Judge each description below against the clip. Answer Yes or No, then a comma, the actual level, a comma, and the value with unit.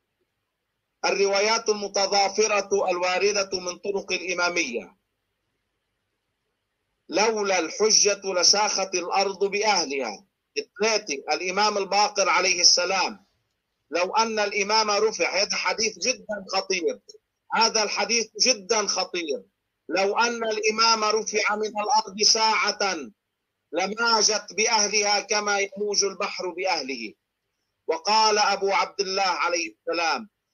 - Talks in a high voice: Yes, high, 205 Hz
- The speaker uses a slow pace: No, average, 90 wpm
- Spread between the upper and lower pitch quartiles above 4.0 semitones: No, narrow, 2.5 semitones